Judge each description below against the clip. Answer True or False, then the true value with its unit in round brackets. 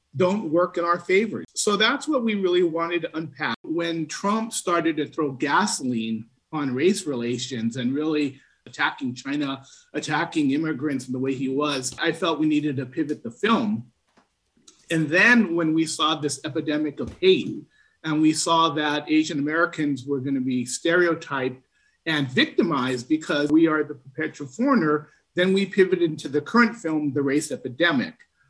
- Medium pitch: True (155 Hz)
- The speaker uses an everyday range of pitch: True (3.5 semitones)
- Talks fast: False (165 wpm)